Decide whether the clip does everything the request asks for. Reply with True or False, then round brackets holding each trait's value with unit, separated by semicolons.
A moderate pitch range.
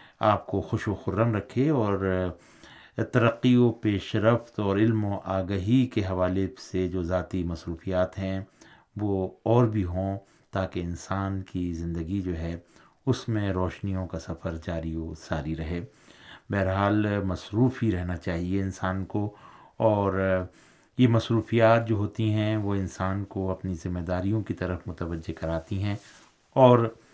True (3.2 semitones)